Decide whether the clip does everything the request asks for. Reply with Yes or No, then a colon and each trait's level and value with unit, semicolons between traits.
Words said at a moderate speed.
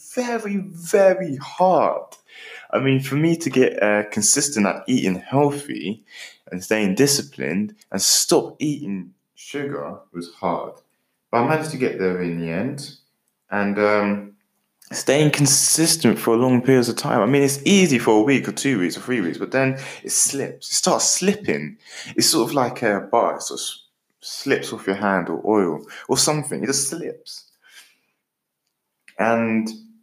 Yes: average, 165 wpm